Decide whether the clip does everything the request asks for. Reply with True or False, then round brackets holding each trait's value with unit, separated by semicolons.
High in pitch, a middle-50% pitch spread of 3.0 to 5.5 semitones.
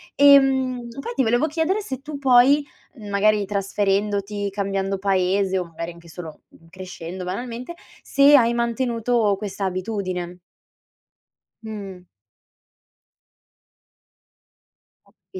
True (205 Hz; 4.9 semitones)